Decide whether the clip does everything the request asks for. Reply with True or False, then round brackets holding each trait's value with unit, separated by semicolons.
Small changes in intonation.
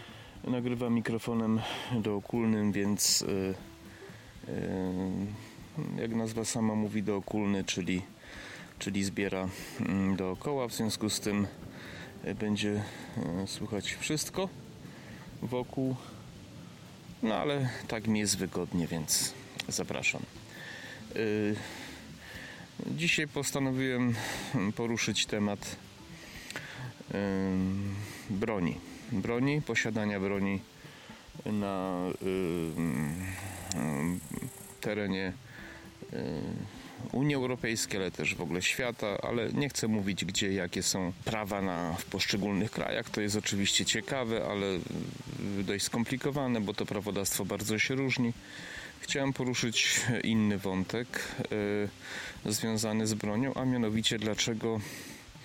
False (3.2 semitones)